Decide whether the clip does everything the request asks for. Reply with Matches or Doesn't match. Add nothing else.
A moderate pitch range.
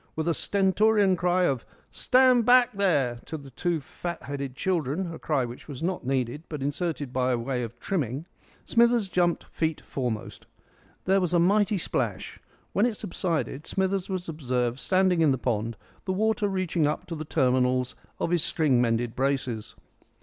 Doesn't match